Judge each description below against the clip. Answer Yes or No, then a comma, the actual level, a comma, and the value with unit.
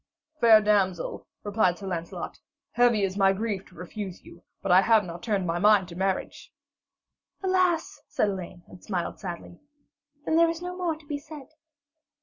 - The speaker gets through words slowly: No, average, 170 wpm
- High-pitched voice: Yes, high, 205 Hz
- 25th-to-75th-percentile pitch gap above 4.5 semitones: Yes, average, 5.0 semitones